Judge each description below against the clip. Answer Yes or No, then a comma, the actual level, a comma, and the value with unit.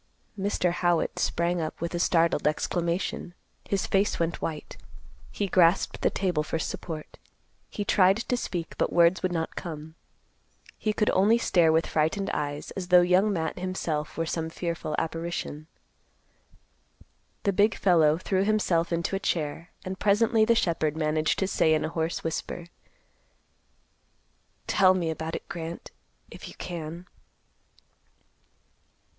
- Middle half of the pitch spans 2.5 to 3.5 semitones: Yes, average, 2.8 semitones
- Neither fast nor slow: Yes, average, 145 wpm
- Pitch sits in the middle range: Yes, medium, 170 Hz